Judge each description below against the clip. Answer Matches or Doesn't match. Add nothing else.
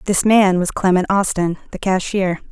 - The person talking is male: Doesn't match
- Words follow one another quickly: Doesn't match